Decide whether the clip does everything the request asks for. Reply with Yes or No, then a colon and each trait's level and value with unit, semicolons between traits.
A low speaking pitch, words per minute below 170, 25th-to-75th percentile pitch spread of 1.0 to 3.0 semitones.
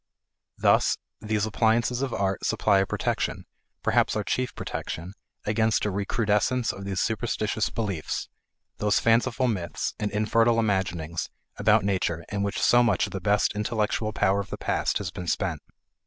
Yes: low, 105 Hz; average, 155 wpm; narrow, 2.6 semitones